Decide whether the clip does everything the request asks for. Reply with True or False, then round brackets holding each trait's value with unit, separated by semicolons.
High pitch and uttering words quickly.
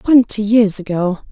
False (210 Hz; 135 wpm)